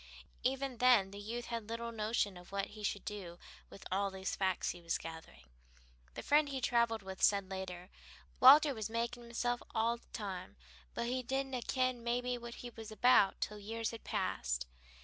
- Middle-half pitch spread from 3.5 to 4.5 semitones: Yes, average, 3.8 semitones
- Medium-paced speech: Yes, average, 185 wpm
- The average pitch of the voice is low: No, high, 225 Hz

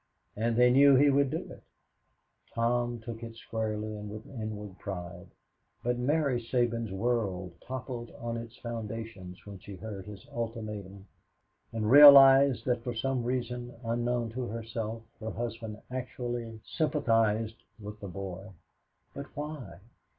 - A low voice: Yes, low, 115 Hz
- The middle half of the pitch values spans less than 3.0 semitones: Yes, narrow, 2.4 semitones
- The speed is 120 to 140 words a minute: Yes, slow, 135 wpm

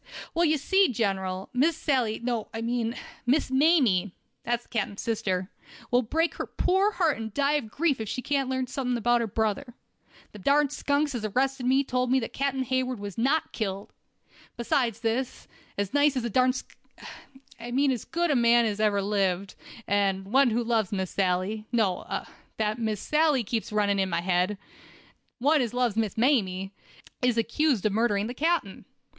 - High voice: Yes, high, 235 Hz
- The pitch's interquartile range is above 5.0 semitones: No, average, 4.5 semitones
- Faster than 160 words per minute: Yes, average, 170 wpm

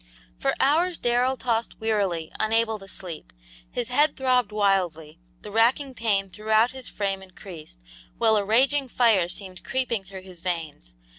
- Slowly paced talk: No, average, 150 wpm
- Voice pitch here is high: Yes, high, 215 Hz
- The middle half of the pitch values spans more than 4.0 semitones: Yes, average, 4.7 semitones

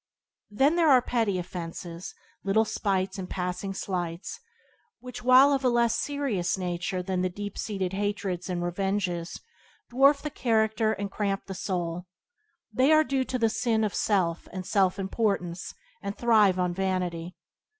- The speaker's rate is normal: Yes, average, 150 wpm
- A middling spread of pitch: Yes, average, 4.1 semitones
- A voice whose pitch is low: No, high, 195 Hz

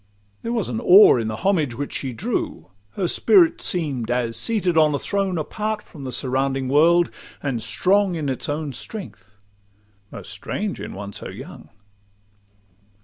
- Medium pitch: Yes, medium, 145 Hz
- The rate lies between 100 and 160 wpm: Yes, average, 150 wpm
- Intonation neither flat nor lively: No, wide, 8.2 semitones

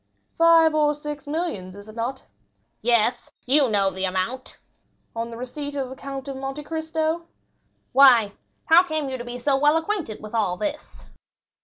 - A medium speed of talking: Yes, average, 170 wpm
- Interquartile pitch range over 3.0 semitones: Yes, average, 4.8 semitones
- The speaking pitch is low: No, very high, 270 Hz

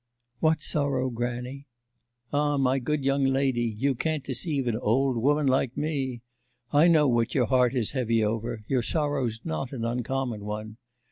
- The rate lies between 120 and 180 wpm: Yes, average, 160 wpm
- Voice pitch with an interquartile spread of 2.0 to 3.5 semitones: Yes, average, 3.2 semitones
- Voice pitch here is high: No, low, 130 Hz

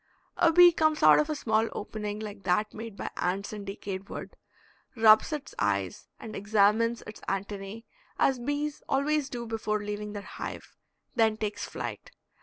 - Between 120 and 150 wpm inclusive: No, average, 165 wpm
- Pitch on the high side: Yes, high, 215 Hz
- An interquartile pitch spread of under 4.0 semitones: No, average, 4.3 semitones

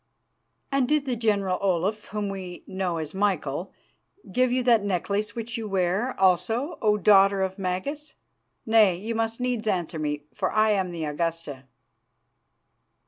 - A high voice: Yes, high, 200 Hz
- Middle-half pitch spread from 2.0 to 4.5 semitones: Yes, average, 3.8 semitones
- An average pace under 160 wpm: Yes, average, 150 wpm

